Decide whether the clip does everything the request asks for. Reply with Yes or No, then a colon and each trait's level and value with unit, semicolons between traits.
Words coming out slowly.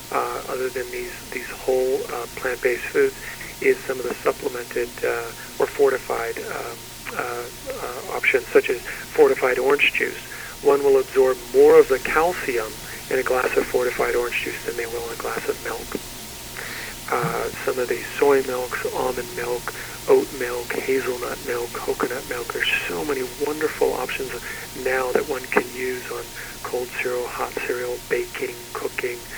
No: average, 160 wpm